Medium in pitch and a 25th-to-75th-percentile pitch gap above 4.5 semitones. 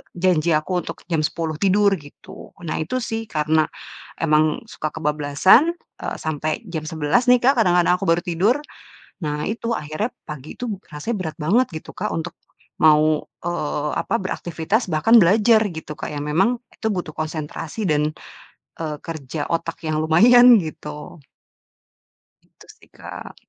Yes: medium, 165 Hz; average, 4.9 semitones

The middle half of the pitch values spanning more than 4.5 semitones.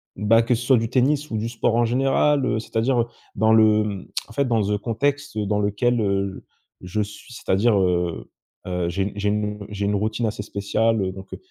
No: average, 2.9 semitones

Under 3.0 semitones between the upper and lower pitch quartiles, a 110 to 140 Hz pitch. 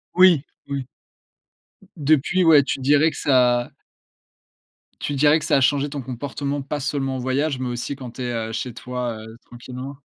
Yes: narrow, 2.6 semitones; low, 135 Hz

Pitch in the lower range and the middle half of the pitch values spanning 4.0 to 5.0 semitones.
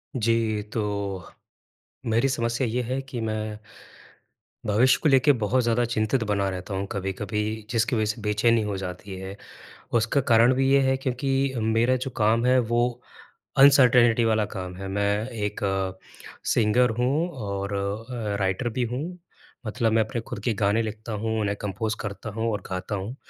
No: low, 110 Hz; average, 3.1 semitones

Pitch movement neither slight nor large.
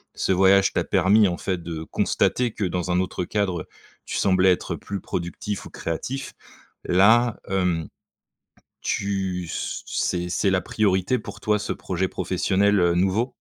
No: narrow, 2.3 semitones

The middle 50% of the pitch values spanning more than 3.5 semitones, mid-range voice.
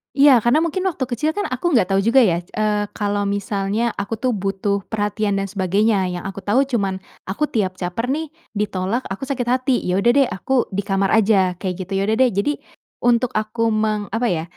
No: average, 3.9 semitones; high, 210 Hz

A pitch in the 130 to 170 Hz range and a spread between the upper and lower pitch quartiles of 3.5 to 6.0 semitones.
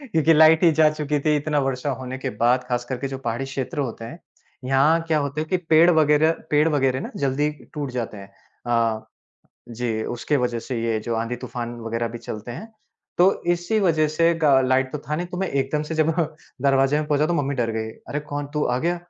Yes: medium, 140 Hz; average, 4.1 semitones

